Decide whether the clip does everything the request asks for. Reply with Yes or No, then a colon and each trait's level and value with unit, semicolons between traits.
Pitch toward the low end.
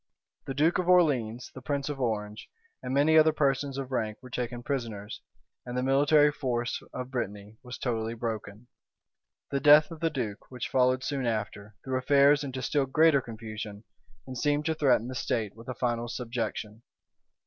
Yes: low, 125 Hz